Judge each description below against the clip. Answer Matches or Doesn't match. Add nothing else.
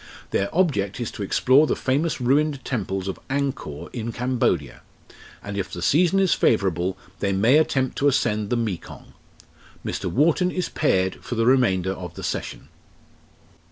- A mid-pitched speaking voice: Doesn't match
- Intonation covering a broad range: Matches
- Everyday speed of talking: Matches